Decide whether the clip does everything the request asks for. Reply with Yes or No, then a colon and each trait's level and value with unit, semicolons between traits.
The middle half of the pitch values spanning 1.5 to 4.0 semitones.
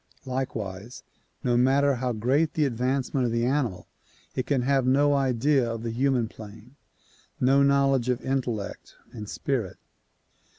Yes: average, 2.7 semitones